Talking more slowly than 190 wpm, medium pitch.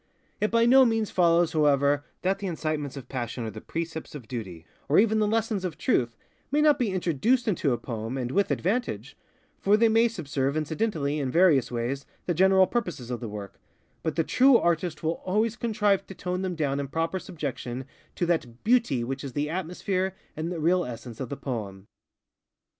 No: average, 195 wpm; medium, 165 Hz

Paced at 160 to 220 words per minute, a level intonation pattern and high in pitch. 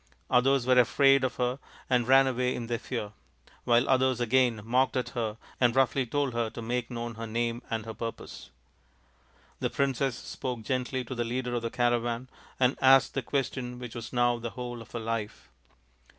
No: average, 190 wpm; narrow, 1.9 semitones; low, 120 Hz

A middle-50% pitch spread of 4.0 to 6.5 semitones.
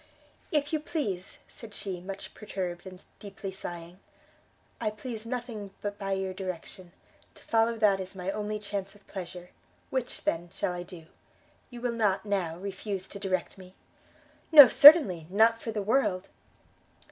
No: average, 3.2 semitones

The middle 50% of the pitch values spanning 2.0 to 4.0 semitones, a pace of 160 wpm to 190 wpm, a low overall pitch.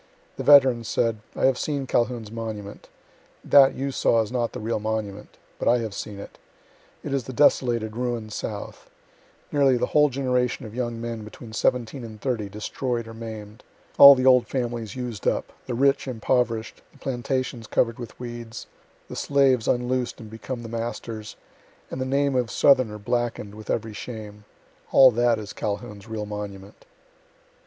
Yes: average, 2.8 semitones; average, 165 wpm; low, 115 Hz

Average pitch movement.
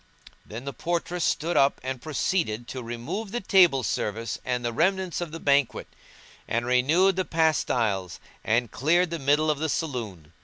No: wide, 6.1 semitones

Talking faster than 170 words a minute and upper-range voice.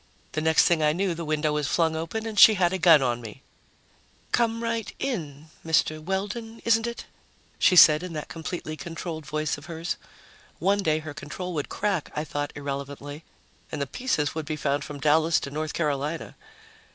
No: average, 190 wpm; medium, 160 Hz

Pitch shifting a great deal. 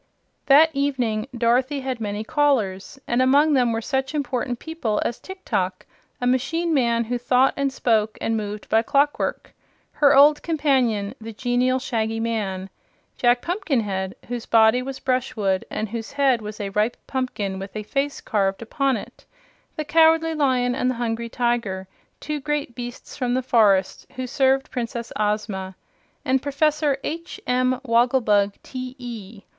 No: average, 3.8 semitones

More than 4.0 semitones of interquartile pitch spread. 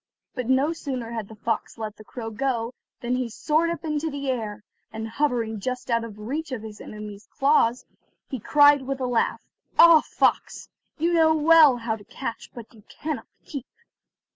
Yes: average, 4.6 semitones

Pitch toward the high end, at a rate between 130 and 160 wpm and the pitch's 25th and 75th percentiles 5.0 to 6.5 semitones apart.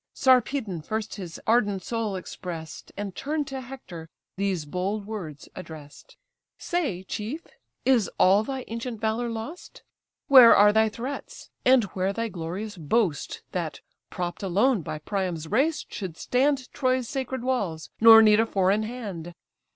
Yes: high, 215 Hz; average, 145 wpm; wide, 5.4 semitones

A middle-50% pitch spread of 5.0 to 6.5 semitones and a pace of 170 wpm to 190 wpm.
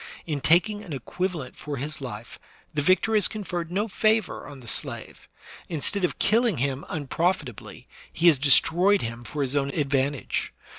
Yes: average, 5.3 semitones; average, 175 wpm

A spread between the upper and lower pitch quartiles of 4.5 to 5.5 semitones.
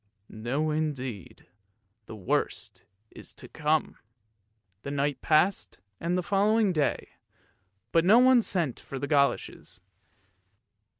Yes: average, 4.9 semitones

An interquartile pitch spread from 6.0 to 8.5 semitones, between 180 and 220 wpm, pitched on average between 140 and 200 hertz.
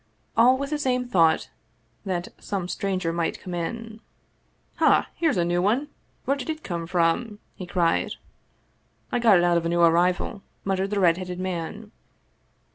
No: average, 4.7 semitones; average, 185 wpm; medium, 185 Hz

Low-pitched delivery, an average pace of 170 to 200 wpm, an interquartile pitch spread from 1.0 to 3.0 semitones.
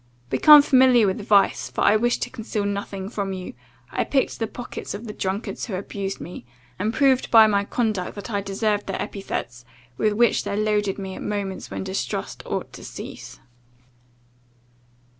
No: high, 205 Hz; average, 175 wpm; narrow, 2.4 semitones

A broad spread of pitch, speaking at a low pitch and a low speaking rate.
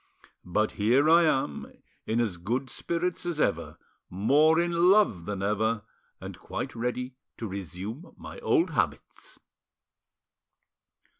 Yes: wide, 8.3 semitones; low, 125 Hz; slow, 125 wpm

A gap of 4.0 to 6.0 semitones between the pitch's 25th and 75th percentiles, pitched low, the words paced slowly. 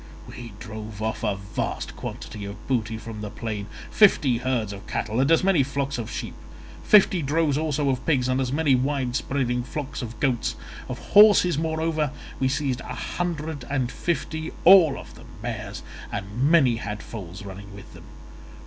No: wide, 5.5 semitones; low, 130 Hz; average, 175 wpm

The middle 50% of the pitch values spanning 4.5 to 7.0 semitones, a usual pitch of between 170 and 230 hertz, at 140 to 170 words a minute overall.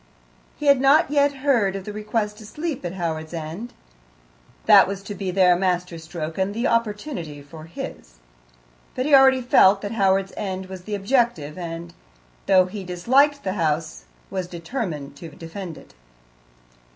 Yes: wide, 5.5 semitones; high, 190 Hz; average, 165 wpm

